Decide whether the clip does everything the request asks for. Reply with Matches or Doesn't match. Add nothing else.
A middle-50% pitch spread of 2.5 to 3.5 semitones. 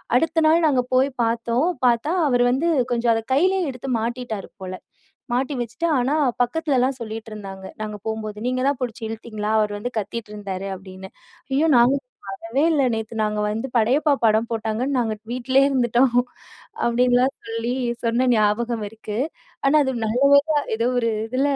Matches